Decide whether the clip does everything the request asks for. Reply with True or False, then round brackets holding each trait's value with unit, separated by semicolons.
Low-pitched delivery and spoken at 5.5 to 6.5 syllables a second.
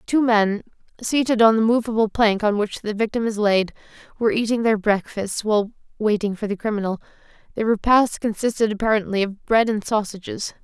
False (215 Hz; 5.6 syllables/s)